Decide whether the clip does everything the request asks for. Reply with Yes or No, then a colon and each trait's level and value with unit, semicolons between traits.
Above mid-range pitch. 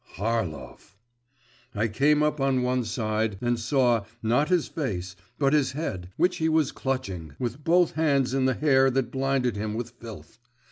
No: low, 125 Hz